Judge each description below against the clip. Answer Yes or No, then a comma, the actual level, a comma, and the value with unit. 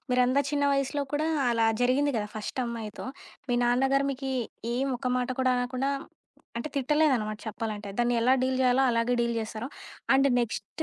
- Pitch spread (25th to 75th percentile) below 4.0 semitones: Yes, narrow, 2.6 semitones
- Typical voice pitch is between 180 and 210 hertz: No, very high, 250 Hz